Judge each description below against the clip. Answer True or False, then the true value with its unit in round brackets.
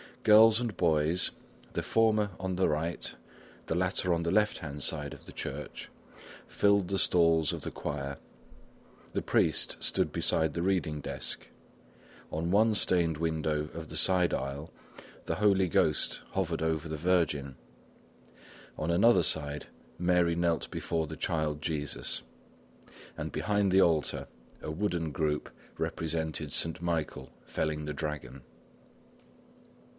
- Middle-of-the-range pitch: False (80 Hz)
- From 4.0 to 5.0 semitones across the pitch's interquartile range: False (3.3 semitones)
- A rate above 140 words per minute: False (135 wpm)